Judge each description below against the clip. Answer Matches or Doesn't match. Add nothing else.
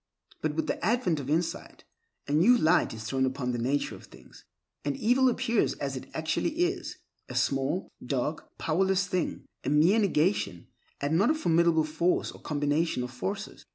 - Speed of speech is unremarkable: Matches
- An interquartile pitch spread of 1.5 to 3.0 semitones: Doesn't match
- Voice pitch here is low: Doesn't match